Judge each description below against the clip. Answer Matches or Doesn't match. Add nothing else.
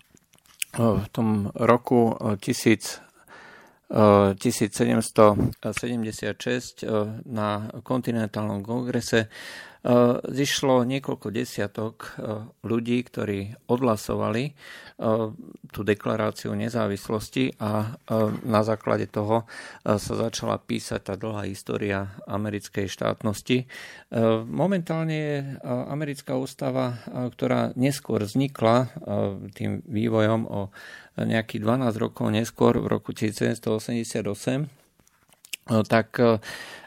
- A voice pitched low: Matches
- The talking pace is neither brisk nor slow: Doesn't match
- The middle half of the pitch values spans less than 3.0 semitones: Matches